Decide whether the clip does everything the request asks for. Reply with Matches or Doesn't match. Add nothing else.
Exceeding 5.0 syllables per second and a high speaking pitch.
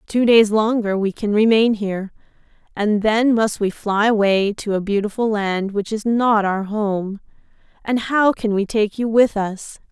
Doesn't match